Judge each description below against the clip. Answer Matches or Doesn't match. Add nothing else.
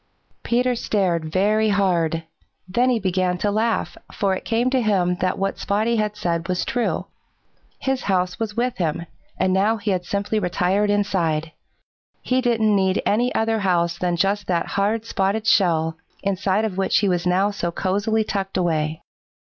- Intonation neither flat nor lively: Matches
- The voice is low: Doesn't match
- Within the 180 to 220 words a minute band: Doesn't match